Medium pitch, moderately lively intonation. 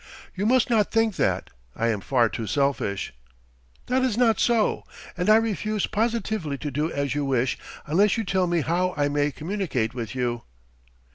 No: medium, 165 Hz; wide, 8.6 semitones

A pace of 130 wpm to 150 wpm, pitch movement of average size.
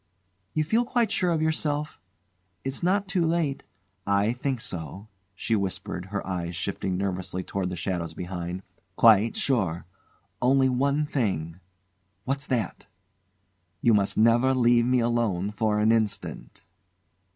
No: average, 140 wpm; wide, 6.4 semitones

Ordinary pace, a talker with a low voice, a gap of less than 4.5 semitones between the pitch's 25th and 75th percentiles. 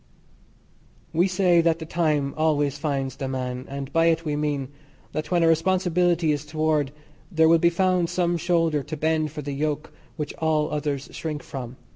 No: average, 180 wpm; medium, 155 Hz; narrow, 2.5 semitones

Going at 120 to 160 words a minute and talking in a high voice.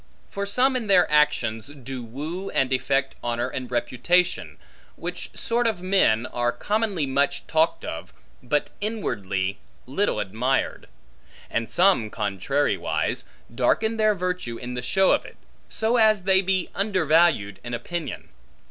No: average, 140 wpm; medium, 150 Hz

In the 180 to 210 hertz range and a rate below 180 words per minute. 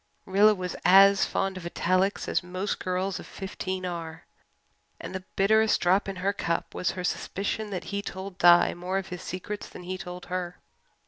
No: medium, 185 Hz; average, 185 wpm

